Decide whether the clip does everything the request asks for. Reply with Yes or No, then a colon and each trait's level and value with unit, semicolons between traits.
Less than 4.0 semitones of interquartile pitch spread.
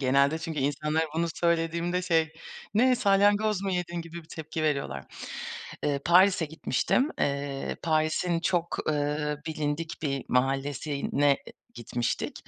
Yes: average, 3.1 semitones